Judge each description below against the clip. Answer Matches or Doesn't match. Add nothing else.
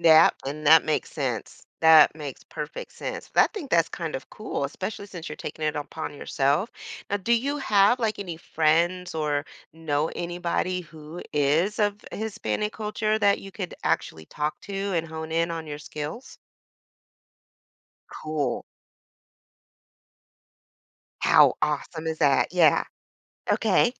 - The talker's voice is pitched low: Doesn't match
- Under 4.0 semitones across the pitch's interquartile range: Doesn't match